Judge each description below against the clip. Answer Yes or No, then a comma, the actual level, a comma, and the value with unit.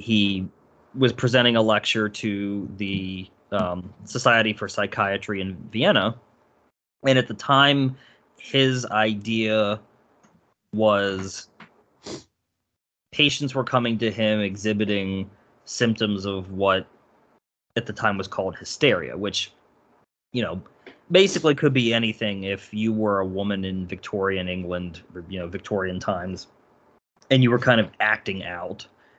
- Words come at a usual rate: No, slow, 125 wpm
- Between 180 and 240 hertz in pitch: No, low, 105 Hz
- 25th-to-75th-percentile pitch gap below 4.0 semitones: Yes, average, 3.3 semitones